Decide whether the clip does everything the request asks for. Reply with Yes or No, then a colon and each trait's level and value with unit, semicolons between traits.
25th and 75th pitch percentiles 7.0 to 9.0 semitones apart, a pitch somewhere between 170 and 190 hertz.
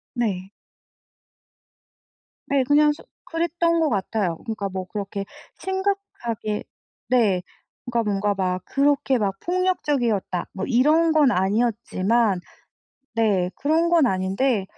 No: wide, 7.3 semitones; high, 235 Hz